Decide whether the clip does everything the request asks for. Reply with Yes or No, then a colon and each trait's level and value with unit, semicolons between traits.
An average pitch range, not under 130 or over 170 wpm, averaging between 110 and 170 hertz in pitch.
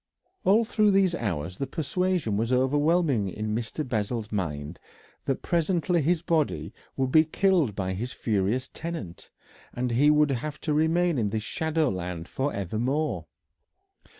No: wide, 7.2 semitones; average, 150 wpm; low, 135 Hz